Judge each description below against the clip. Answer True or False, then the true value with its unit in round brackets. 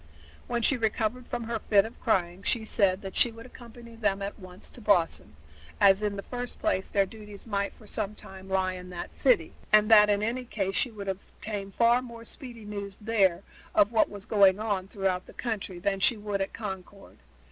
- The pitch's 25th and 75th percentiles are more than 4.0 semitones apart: False (2.9 semitones)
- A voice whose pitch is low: False (205 Hz)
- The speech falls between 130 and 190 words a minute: False (205 wpm)